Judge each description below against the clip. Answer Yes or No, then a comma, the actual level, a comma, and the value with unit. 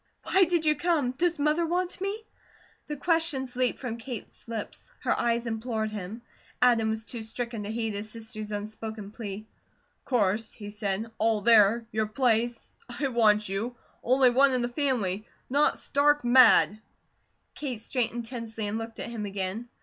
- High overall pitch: Yes, high, 230 Hz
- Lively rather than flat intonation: No, average, 3.4 semitones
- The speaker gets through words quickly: No, average, 165 wpm